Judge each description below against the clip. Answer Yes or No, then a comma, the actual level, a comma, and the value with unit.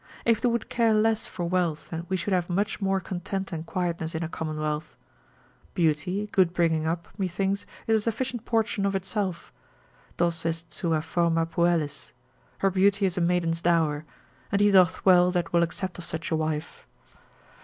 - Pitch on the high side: No, medium, 175 Hz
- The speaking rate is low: No, average, 175 wpm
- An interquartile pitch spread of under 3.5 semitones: Yes, average, 3.0 semitones